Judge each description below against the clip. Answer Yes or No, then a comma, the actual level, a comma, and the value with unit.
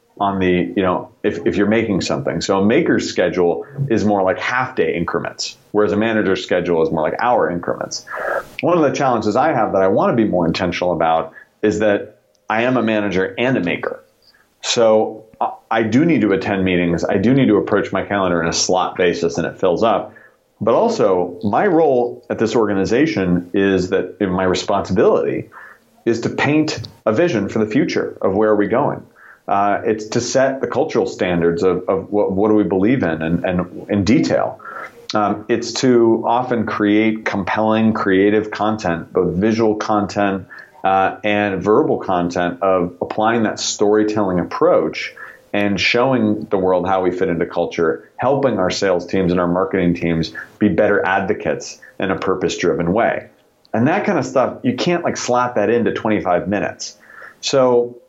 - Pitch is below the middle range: Yes, low, 100 Hz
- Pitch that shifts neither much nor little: Yes, average, 3.2 semitones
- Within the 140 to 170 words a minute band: No, average, 180 wpm